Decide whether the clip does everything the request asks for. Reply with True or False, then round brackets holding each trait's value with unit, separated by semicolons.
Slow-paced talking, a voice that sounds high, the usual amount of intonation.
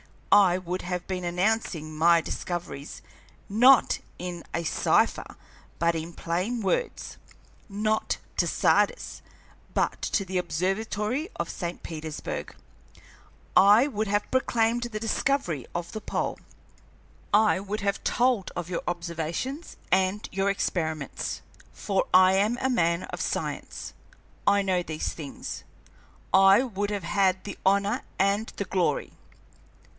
True (130 wpm; 195 Hz; 3.7 semitones)